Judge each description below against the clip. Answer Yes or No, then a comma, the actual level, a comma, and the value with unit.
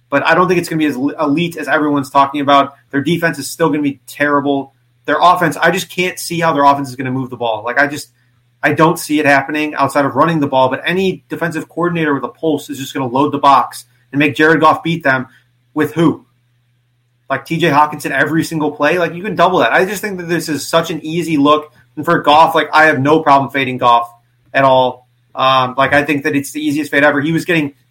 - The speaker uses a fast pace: Yes, fast, 250 wpm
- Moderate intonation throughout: Yes, average, 3.1 semitones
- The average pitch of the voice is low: No, medium, 145 Hz